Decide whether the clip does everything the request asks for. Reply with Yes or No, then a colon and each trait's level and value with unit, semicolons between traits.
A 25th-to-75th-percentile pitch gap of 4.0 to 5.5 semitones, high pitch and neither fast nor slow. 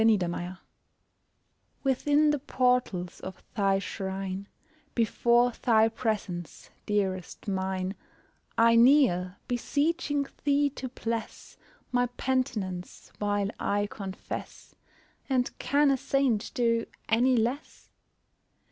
No: average, 5.0 semitones; high, 230 Hz; slow, 95 wpm